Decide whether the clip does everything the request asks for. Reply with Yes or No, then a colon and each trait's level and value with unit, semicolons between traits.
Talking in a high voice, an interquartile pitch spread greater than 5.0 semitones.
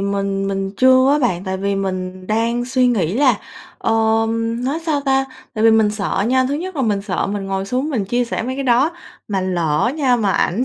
No: high, 225 Hz; average, 4.7 semitones